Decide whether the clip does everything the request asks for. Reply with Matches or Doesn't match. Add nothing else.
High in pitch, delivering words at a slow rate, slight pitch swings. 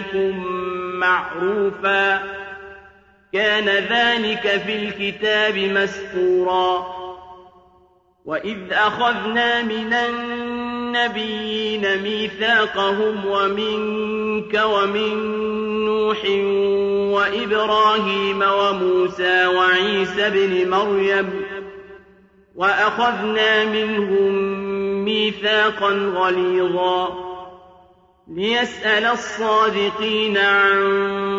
Matches